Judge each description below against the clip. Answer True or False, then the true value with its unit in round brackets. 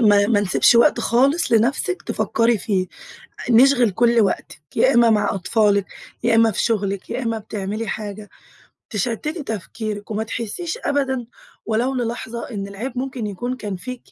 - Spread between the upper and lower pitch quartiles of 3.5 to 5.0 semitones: False (3.0 semitones)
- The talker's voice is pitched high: True (225 Hz)